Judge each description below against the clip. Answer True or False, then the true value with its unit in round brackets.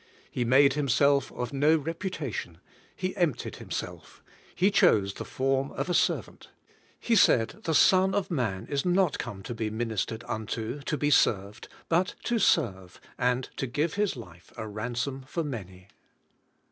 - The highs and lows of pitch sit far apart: True (6.6 semitones)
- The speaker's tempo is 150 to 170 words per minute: True (160 wpm)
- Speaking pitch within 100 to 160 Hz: True (135 Hz)